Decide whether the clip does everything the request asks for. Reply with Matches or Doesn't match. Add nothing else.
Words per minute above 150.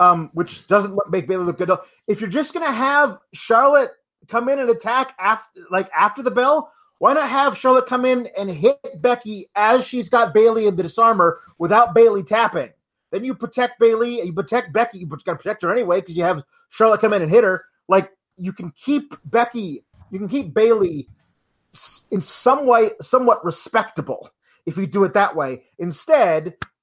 Matches